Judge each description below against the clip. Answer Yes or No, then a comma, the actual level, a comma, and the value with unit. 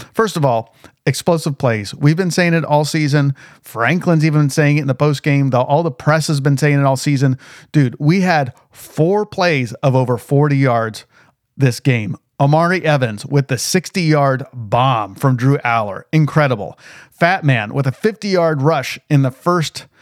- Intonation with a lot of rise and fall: No, average, 3.1 semitones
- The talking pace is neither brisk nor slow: Yes, average, 175 wpm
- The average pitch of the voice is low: No, medium, 145 Hz